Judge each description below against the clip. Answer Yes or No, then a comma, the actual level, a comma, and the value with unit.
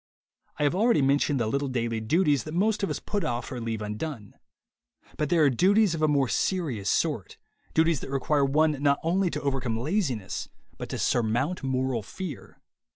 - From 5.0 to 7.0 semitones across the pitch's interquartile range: Yes, average, 5.3 semitones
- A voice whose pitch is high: No, medium, 140 Hz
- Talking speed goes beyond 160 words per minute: Yes, average, 185 wpm